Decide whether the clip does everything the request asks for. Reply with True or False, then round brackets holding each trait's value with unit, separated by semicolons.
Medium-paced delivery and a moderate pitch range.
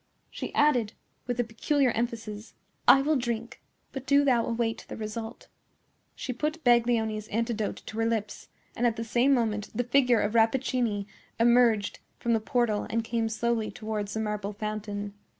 False (165 wpm; 2.2 semitones)